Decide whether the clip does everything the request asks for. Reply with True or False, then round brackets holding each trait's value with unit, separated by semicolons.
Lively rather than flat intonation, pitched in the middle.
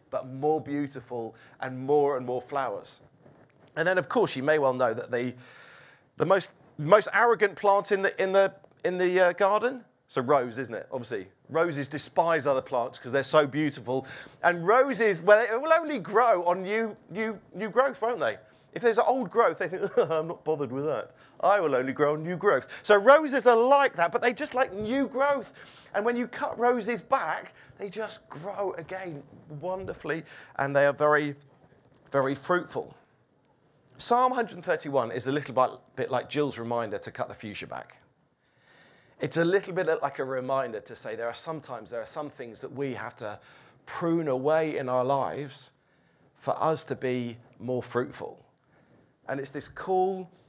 True (7.0 semitones; 155 Hz)